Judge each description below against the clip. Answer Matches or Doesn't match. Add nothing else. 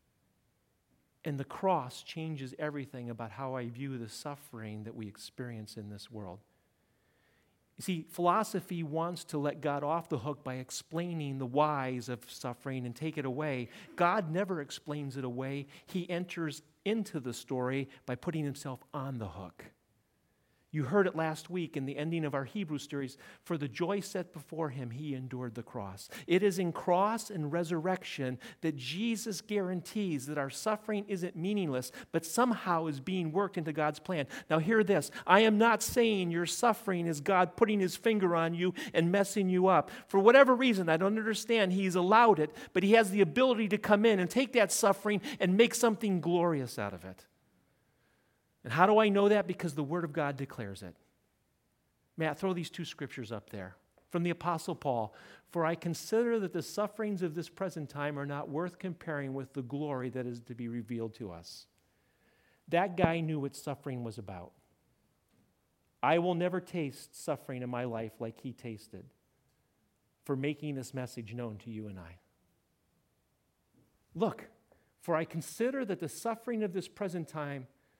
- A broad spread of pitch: Matches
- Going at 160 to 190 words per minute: Matches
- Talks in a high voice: Doesn't match